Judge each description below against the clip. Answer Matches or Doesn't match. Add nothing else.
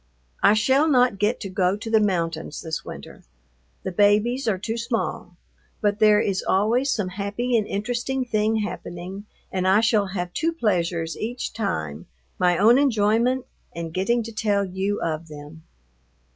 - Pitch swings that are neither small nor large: Matches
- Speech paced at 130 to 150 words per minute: Doesn't match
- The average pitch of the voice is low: Doesn't match